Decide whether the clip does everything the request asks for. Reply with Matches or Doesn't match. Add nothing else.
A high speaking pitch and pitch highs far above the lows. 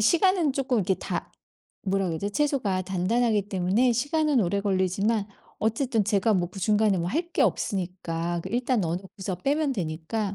Doesn't match